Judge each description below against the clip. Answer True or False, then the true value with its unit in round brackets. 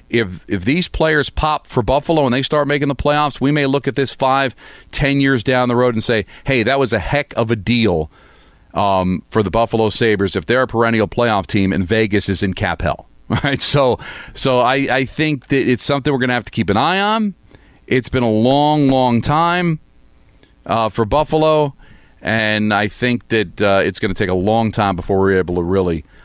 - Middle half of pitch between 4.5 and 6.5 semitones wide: True (5.1 semitones)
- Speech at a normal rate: False (215 wpm)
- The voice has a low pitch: True (120 Hz)